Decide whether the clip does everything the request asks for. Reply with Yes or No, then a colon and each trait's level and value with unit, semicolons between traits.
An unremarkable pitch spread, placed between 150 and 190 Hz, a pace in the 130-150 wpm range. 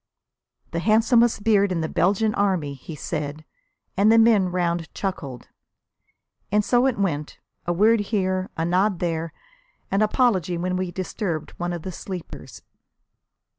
Yes: average, 3.8 semitones; medium, 185 Hz; average, 145 wpm